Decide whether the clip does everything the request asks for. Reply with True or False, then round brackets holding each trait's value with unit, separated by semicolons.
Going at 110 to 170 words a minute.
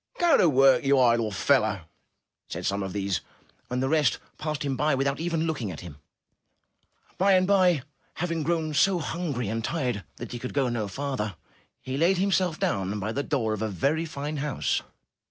False (190 wpm)